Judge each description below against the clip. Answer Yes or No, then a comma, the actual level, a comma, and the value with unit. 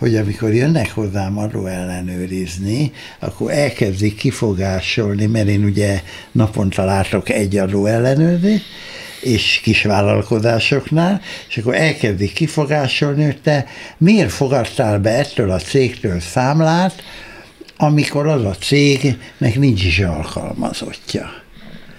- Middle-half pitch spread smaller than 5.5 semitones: No, wide, 6.1 semitones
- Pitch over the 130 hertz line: No, low, 115 Hz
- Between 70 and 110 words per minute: Yes, slow, 105 wpm